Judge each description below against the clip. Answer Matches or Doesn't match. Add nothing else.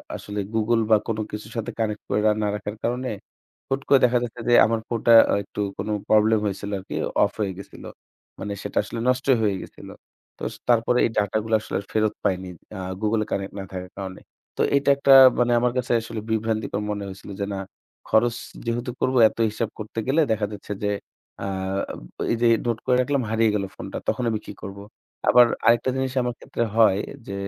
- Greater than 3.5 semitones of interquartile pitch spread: Doesn't match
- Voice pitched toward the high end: Doesn't match